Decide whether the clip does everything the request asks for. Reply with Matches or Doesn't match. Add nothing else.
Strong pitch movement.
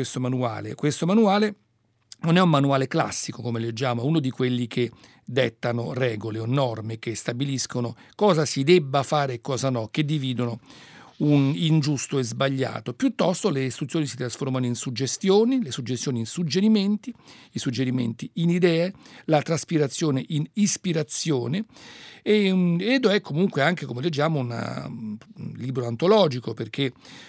Matches